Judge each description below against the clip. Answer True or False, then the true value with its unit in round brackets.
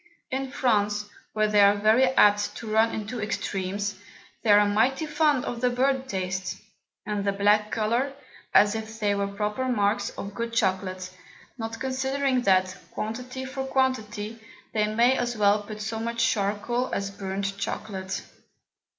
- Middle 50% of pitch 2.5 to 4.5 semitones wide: True (3.4 semitones)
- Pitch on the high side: True (215 Hz)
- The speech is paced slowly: False (155 wpm)